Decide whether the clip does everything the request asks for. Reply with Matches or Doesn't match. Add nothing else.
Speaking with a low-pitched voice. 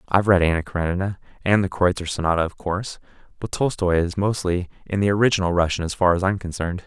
Matches